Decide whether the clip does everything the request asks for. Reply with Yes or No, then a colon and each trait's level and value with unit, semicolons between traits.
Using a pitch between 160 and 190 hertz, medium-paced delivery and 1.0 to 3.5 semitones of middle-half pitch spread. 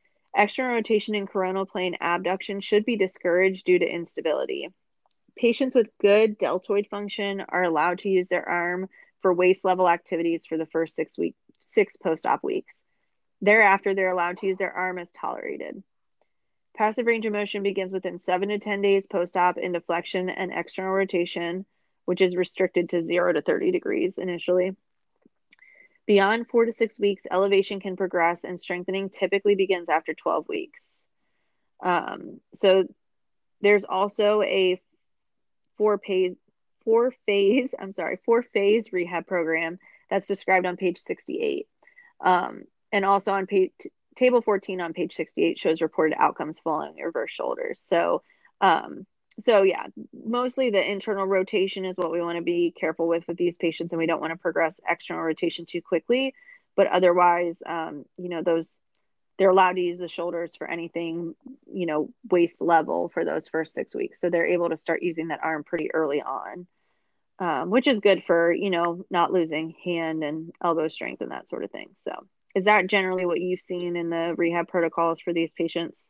Yes: medium, 185 Hz; average, 170 wpm; average, 3.2 semitones